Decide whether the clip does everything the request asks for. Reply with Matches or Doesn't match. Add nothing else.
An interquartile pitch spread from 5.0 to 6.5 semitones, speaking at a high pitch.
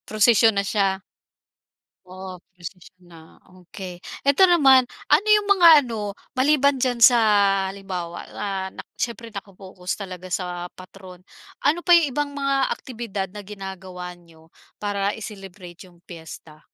Matches